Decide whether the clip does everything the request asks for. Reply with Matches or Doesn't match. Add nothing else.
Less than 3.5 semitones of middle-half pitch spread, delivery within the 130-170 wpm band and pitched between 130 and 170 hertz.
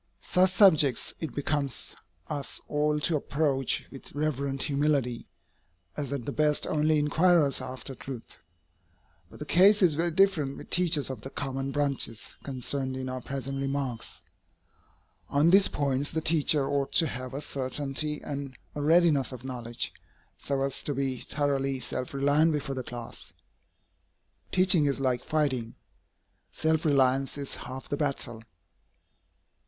Matches